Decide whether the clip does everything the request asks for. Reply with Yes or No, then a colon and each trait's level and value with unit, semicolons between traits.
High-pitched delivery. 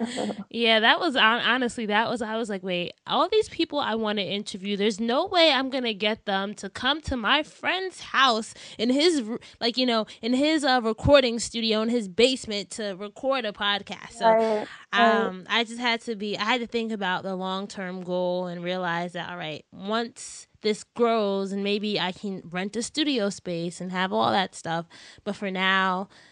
Yes: high, 215 Hz